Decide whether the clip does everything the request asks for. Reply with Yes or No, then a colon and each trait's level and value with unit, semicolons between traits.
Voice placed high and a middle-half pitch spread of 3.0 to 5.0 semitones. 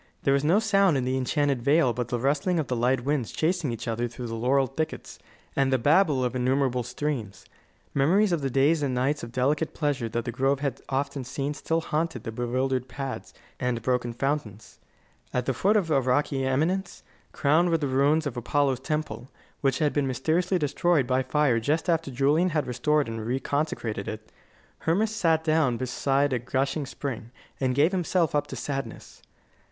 No: low, 135 Hz; average, 3.6 semitones